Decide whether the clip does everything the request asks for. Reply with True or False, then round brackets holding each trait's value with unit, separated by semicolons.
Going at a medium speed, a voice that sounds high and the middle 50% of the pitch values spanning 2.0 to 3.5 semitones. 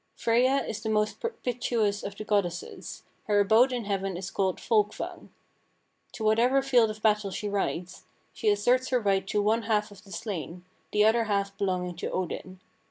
True (175 wpm; 210 Hz; 2.6 semitones)